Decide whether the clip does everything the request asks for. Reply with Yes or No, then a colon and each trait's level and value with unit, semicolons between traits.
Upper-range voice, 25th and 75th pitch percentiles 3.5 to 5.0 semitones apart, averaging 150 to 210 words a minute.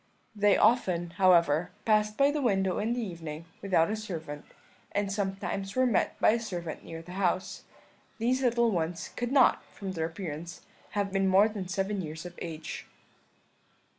Yes: high, 195 Hz; average, 4.0 semitones; average, 165 wpm